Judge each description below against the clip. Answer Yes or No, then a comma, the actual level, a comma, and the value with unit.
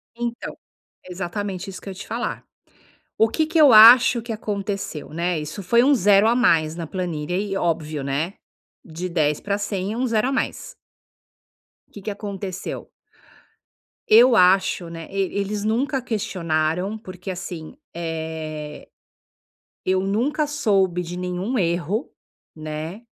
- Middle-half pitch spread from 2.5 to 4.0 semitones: No, average, 4.5 semitones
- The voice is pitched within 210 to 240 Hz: No, high, 190 Hz